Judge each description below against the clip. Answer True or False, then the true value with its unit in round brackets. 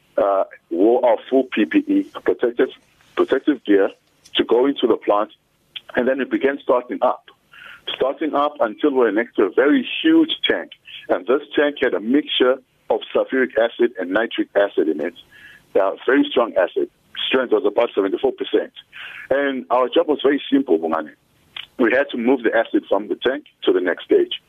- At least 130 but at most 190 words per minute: True (175 wpm)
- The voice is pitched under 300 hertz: False (325 Hz)